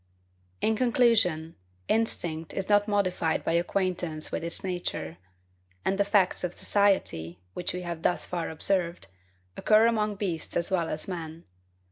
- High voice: No, medium, 180 Hz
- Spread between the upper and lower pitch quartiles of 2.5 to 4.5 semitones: Yes, average, 3.7 semitones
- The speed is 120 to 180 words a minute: Yes, average, 145 wpm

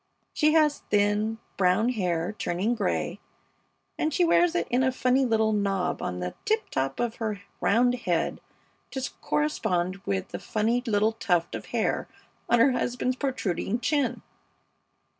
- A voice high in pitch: Yes, high, 225 Hz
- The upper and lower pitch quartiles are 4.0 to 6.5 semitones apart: Yes, average, 4.9 semitones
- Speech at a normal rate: Yes, average, 150 wpm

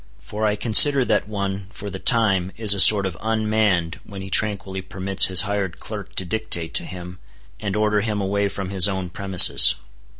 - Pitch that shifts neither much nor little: No, narrow, 2.1 semitones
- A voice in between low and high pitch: No, low, 100 Hz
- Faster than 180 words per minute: Yes, average, 190 wpm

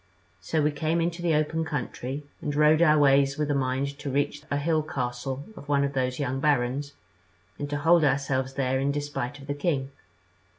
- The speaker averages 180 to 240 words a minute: Yes, average, 200 wpm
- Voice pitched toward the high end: No, medium, 145 Hz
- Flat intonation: Yes, narrow, 2.0 semitones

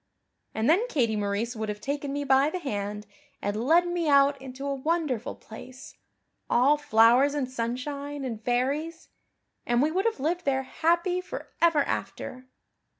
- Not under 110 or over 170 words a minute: Yes, average, 160 wpm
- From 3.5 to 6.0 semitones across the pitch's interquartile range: Yes, average, 4.3 semitones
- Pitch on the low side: No, very high, 275 Hz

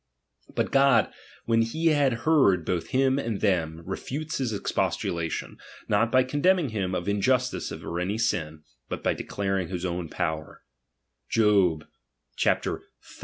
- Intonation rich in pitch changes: Yes, wide, 6.8 semitones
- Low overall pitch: Yes, low, 100 Hz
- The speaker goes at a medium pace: No, slow, 130 wpm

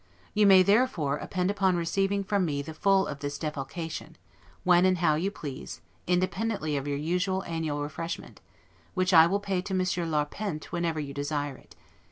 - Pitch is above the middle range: No, medium, 170 Hz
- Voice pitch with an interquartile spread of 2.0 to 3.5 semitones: No, average, 4.0 semitones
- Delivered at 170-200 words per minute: Yes, average, 175 wpm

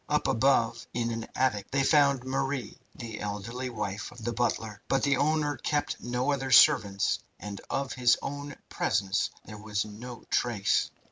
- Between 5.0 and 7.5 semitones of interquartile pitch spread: No, average, 4.2 semitones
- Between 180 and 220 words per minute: No, average, 160 wpm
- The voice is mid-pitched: No, low, 120 Hz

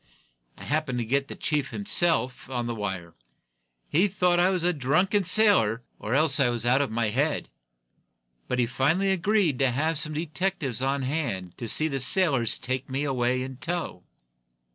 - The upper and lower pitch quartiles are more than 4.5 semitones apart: Yes, average, 5.3 semitones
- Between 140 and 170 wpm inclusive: No, average, 185 wpm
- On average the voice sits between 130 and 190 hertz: Yes, medium, 140 Hz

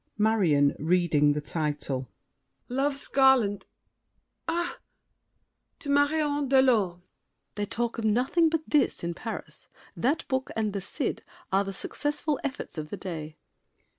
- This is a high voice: Yes, high, 220 Hz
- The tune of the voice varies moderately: No, wide, 8.5 semitones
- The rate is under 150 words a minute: Yes, slow, 135 wpm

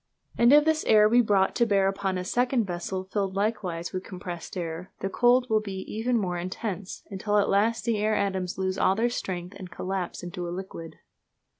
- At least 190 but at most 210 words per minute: Yes, average, 200 wpm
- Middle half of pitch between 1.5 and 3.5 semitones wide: Yes, average, 3.1 semitones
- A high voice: Yes, high, 195 Hz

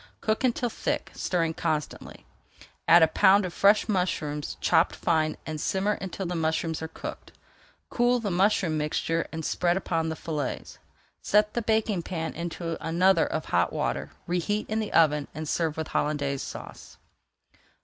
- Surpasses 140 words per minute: Yes, average, 160 wpm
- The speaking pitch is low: No, medium, 170 Hz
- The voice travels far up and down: No, average, 3.8 semitones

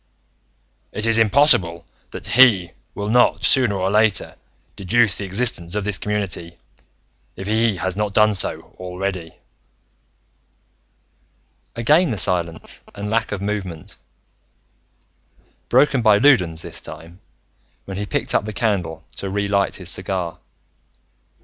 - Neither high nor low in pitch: No, low, 100 Hz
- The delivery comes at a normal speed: No, slow, 130 wpm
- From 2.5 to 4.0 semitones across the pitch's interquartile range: Yes, average, 3.4 semitones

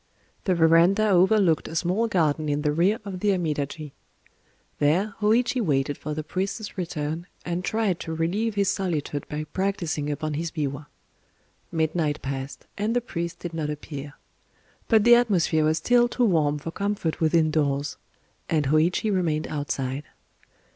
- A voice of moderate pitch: Yes, medium, 165 Hz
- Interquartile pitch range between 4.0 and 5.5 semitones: Yes, average, 4.7 semitones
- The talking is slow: No, average, 155 wpm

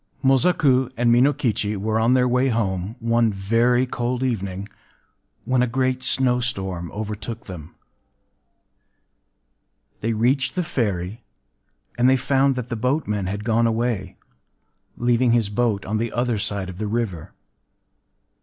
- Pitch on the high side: No, low, 115 Hz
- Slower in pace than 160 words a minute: Yes, slow, 135 wpm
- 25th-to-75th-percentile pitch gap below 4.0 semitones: Yes, average, 3.5 semitones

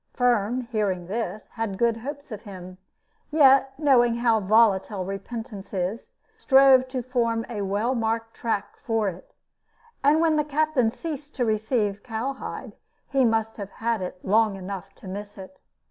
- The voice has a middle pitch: No, high, 225 Hz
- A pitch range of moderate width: Yes, average, 4.2 semitones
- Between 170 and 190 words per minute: No, average, 160 wpm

